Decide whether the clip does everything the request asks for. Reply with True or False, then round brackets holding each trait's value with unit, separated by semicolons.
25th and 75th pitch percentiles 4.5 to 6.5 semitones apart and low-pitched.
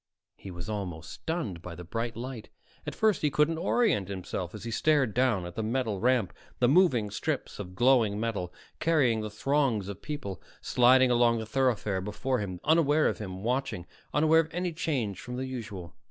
True (5.3 semitones; 115 Hz)